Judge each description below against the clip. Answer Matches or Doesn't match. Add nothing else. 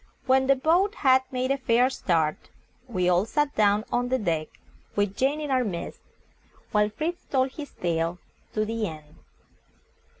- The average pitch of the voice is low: Doesn't match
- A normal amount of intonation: Doesn't match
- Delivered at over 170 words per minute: Doesn't match